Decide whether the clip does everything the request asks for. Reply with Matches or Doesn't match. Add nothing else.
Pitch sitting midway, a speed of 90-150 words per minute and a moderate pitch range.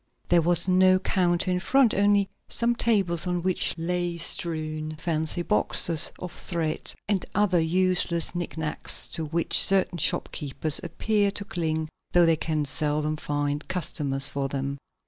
Matches